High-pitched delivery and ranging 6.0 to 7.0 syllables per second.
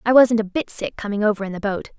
Yes: high, 215 Hz; 6.5 syllables/s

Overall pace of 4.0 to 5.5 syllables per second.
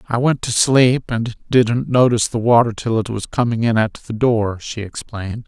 Yes: 4.9 syllables/s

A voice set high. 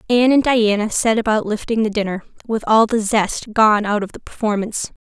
Yes: high, 215 Hz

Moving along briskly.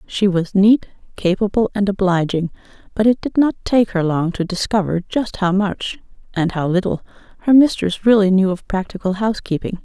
No: average, 160 wpm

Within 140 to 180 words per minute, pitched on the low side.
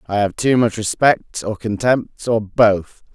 Yes: average, 170 wpm; low, 110 Hz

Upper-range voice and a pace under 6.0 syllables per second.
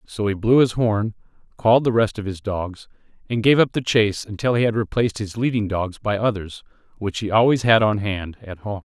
No: low, 105 Hz; 5.5 syllables/s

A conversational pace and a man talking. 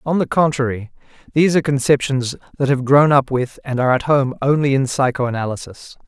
Yes: average, 180 wpm; male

